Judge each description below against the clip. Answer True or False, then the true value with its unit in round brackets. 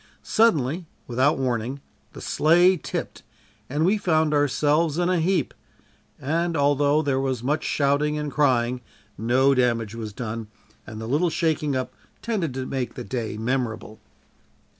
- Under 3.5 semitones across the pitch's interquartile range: False (4.1 semitones)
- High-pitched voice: False (140 Hz)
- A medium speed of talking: True (145 wpm)